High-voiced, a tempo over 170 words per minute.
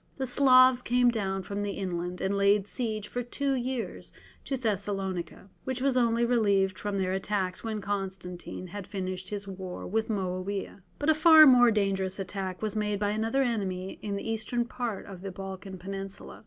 Yes: high, 205 Hz; average, 180 wpm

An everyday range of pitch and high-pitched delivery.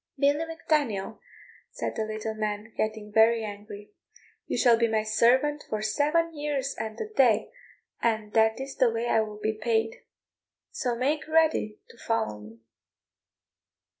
Yes: average, 4.2 semitones; high, 225 Hz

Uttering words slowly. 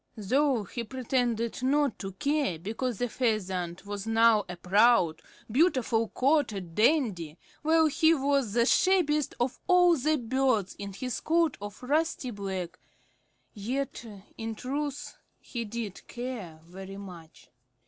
Yes: slow, 130 wpm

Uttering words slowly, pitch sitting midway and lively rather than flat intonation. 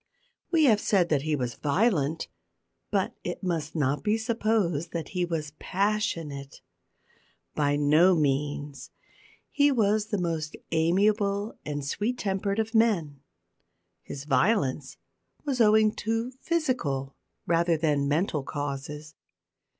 Yes: slow, 120 wpm; medium, 170 Hz; wide, 6.5 semitones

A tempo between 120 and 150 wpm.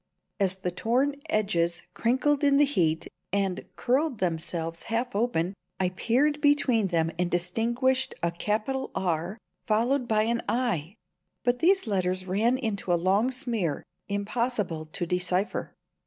Yes: average, 140 wpm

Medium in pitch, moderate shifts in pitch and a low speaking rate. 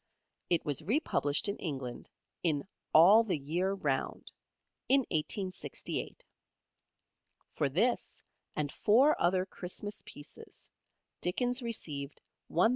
No: medium, 180 Hz; wide, 6.4 semitones; slow, 105 wpm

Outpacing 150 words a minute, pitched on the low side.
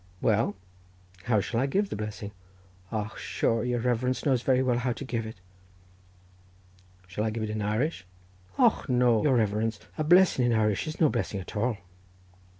Yes: average, 170 wpm; low, 115 Hz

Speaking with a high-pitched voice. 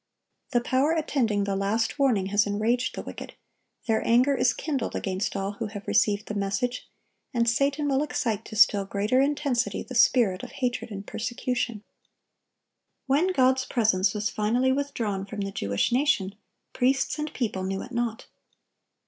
Yes: high, 235 Hz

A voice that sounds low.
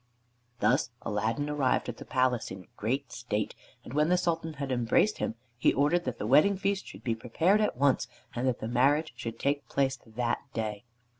Yes: low, 130 Hz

